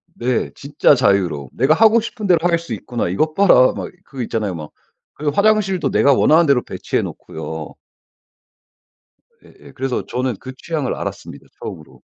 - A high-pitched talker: No, medium, 140 Hz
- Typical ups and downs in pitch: No, wide, 6.0 semitones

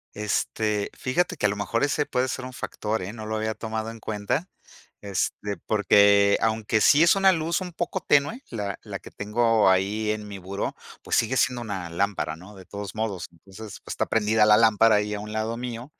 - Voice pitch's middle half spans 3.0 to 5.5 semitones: No, narrow, 2.5 semitones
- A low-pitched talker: Yes, low, 110 Hz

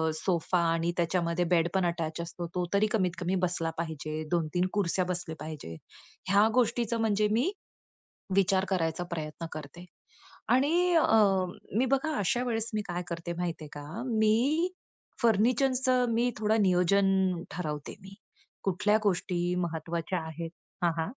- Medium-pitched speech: Yes, medium, 180 Hz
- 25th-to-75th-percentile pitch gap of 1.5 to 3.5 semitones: No, average, 4.6 semitones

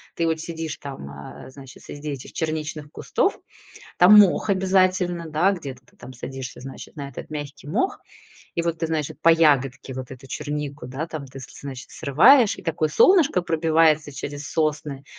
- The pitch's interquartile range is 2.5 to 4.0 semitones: Yes, average, 3.3 semitones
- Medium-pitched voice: Yes, medium, 150 Hz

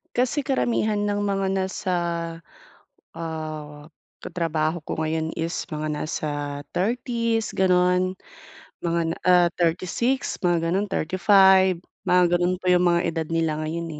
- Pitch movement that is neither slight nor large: Yes, average, 3.1 semitones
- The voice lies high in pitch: No, medium, 180 Hz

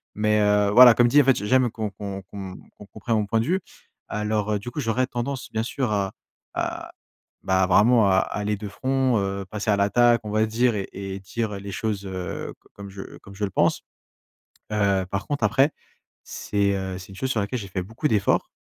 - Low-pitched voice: Yes, low, 105 Hz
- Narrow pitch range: No, average, 3.2 semitones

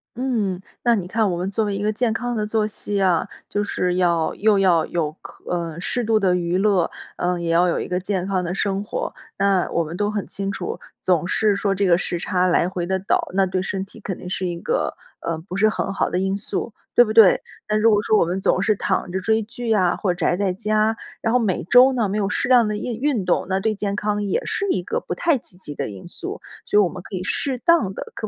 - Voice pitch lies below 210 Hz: Yes, high, 195 Hz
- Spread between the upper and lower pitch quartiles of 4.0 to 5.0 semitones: No, average, 3.0 semitones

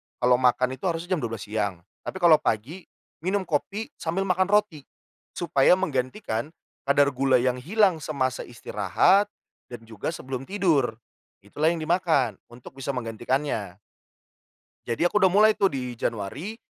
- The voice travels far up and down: Yes, wide, 6.8 semitones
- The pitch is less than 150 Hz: Yes, medium, 140 Hz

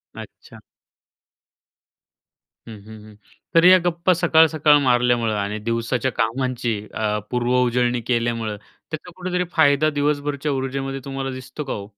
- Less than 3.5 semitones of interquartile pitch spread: No, average, 4.2 semitones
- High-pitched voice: No, low, 130 Hz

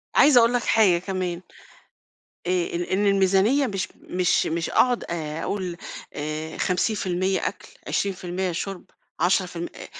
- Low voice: No, medium, 185 Hz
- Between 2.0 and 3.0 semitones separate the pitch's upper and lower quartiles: Yes, narrow, 2.4 semitones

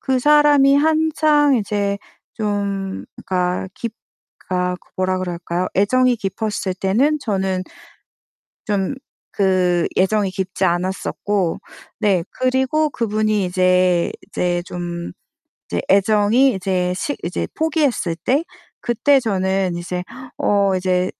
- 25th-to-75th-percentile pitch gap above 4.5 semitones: Yes, average, 5.3 semitones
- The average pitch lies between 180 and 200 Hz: Yes, high, 195 Hz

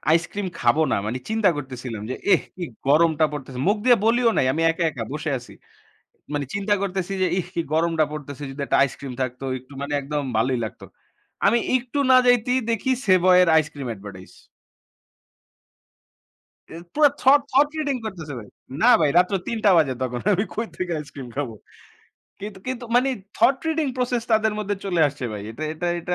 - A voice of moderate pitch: Yes, medium, 170 Hz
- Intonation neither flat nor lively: No, wide, 8.2 semitones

